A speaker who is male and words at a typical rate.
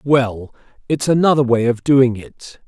Yes: male; average, 155 wpm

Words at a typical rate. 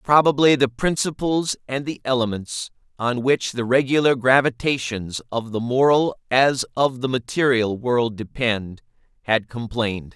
No: slow, 130 wpm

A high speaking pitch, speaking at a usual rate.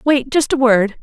Yes: very high, 255 Hz; average, 175 wpm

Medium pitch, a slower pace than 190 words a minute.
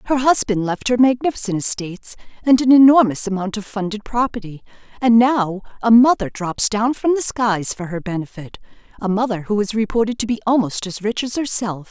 No: high, 220 Hz; average, 180 wpm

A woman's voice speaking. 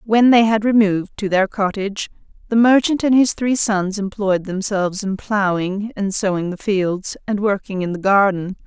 Yes: female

